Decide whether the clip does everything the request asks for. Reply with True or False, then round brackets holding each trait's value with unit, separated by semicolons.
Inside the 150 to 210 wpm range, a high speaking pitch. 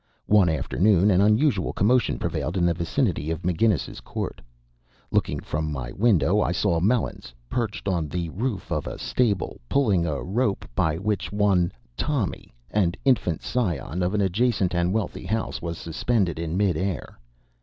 False (165 wpm; 95 Hz)